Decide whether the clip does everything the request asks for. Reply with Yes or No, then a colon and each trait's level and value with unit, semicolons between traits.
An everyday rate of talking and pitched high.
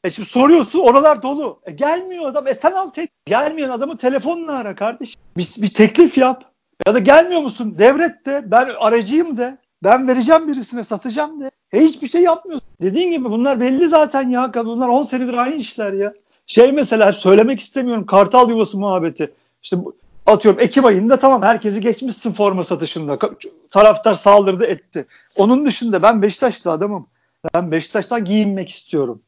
No: fast, 165 wpm; high, 245 Hz